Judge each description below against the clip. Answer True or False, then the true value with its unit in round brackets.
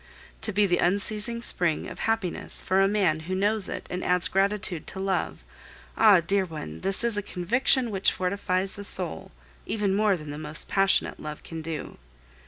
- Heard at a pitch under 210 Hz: True (190 Hz)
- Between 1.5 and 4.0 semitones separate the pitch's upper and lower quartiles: True (2.9 semitones)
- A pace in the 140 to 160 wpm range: False (185 wpm)